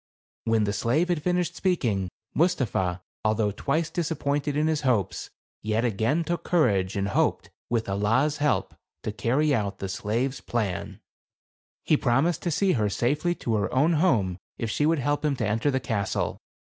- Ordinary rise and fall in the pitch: No, wide, 6.4 semitones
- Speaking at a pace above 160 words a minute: Yes, average, 170 wpm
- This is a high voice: No, low, 130 Hz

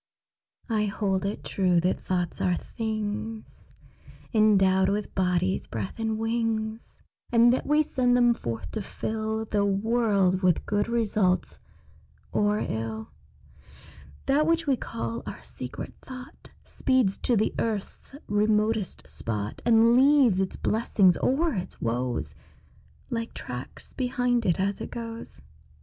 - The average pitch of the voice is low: No, high, 215 Hz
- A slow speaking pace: Yes, slow, 130 wpm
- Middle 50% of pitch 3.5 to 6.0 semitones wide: Yes, average, 3.8 semitones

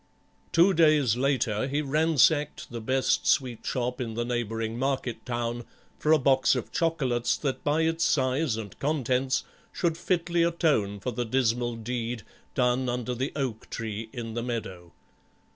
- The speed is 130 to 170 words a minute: Yes, average, 155 wpm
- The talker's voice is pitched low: Yes, low, 125 Hz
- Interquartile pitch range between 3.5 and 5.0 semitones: Yes, average, 4.0 semitones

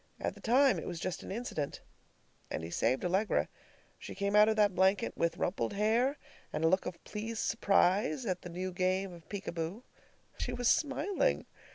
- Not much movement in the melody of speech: No, average, 4.0 semitones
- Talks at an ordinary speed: Yes, average, 195 wpm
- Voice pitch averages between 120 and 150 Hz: No, high, 195 Hz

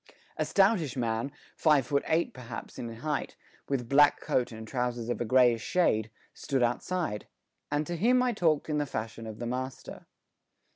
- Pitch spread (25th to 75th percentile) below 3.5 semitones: No, average, 4.7 semitones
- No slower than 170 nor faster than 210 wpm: Yes, average, 175 wpm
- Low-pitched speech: Yes, low, 130 Hz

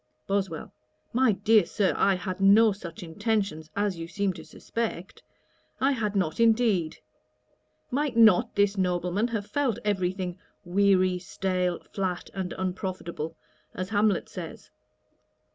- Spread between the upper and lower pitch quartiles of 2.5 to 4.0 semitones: Yes, average, 2.8 semitones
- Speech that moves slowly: Yes, slow, 130 wpm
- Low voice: No, high, 195 Hz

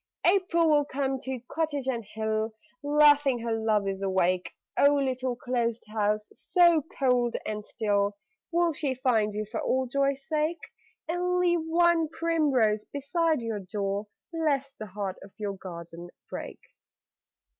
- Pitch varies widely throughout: Yes, wide, 6.1 semitones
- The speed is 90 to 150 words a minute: Yes, average, 140 wpm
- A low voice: No, very high, 255 Hz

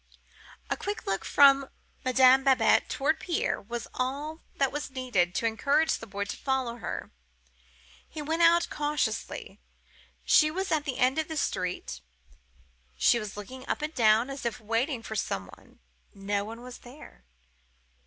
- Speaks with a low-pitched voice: No, very high, 255 Hz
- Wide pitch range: No, average, 4.9 semitones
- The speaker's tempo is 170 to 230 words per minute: No, average, 155 wpm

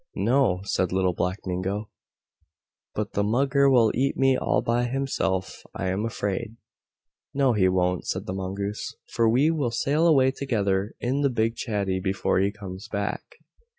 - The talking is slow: No, average, 160 wpm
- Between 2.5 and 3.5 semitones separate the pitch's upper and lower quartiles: No, average, 5.3 semitones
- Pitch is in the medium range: No, low, 105 Hz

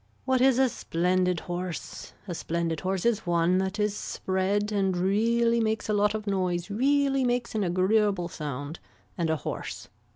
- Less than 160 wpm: No, average, 165 wpm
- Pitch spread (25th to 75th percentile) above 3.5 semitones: Yes, average, 3.9 semitones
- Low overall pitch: No, high, 195 Hz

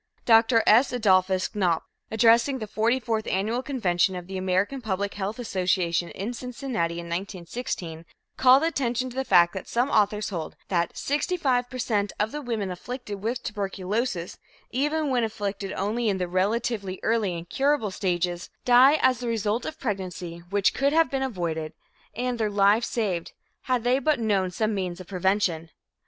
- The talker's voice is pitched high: Yes, high, 210 Hz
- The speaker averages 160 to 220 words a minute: Yes, average, 170 wpm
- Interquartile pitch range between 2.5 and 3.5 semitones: No, average, 4.8 semitones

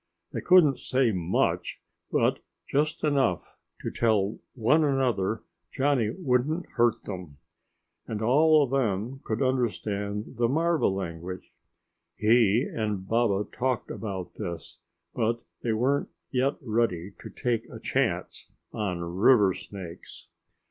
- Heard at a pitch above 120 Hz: No, low, 115 Hz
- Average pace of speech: No, slow, 120 wpm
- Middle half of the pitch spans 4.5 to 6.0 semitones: Yes, average, 5.1 semitones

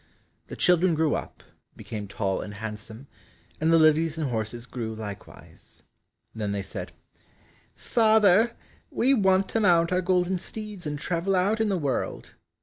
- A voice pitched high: No, medium, 165 Hz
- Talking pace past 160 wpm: No, average, 150 wpm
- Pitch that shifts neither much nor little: No, wide, 9.0 semitones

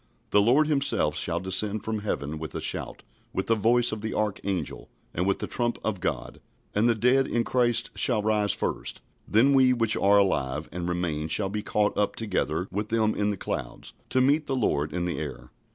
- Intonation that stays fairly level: No, average, 4.8 semitones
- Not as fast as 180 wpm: No, fast, 205 wpm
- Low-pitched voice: Yes, low, 105 Hz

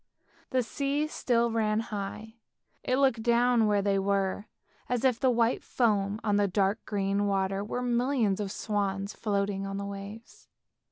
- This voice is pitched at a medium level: No, high, 210 Hz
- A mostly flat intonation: No, average, 3.1 semitones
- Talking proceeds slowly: No, average, 160 wpm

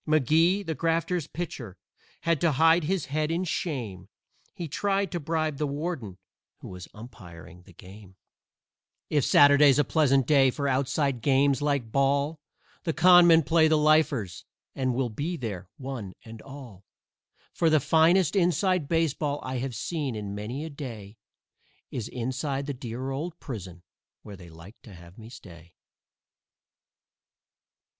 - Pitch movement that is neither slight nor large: No, wide, 6.0 semitones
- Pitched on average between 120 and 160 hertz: Yes, medium, 140 Hz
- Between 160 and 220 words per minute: No, average, 150 wpm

